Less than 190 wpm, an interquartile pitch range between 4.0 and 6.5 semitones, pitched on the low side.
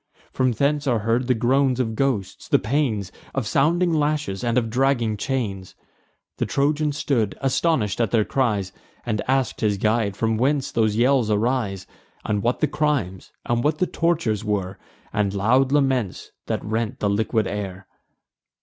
Yes: average, 160 wpm; average, 4.6 semitones; low, 120 Hz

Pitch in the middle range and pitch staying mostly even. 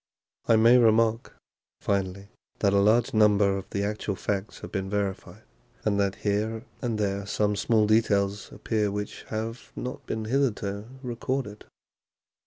No: low, 105 Hz; narrow, 2.0 semitones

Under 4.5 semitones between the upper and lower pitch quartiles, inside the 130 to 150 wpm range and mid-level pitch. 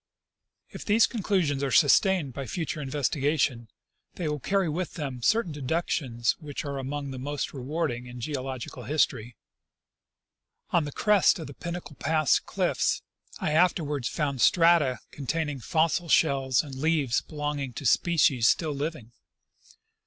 Yes: average, 3.7 semitones; average, 145 wpm; medium, 145 Hz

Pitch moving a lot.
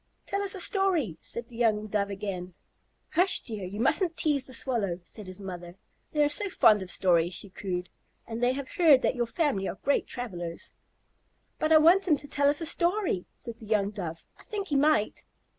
Yes: wide, 7.8 semitones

